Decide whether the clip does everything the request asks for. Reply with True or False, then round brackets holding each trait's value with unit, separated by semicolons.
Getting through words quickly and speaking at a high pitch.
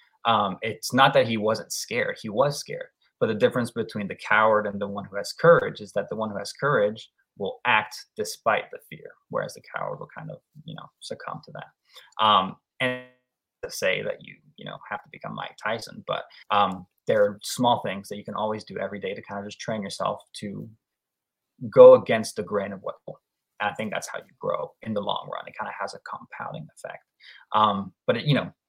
False (225 wpm; 125 Hz)